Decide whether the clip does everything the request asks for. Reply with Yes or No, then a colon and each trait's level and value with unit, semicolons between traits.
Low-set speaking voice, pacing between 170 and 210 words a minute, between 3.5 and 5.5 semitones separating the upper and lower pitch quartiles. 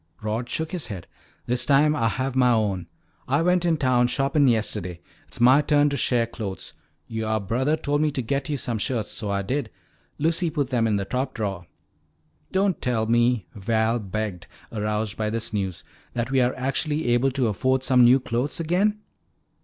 Yes: low, 125 Hz; average, 185 wpm; average, 4.4 semitones